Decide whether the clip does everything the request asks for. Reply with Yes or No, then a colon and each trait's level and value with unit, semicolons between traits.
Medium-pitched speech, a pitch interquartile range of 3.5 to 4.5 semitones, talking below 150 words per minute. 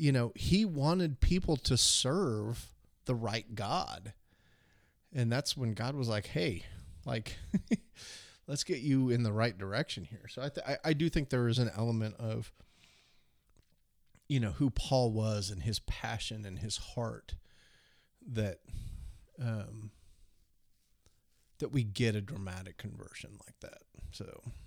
No: low, 115 Hz; average, 4.1 semitones; average, 140 wpm